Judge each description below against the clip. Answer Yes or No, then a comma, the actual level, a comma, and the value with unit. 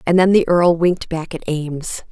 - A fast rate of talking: Yes, fast, 225 wpm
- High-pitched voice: No, medium, 170 Hz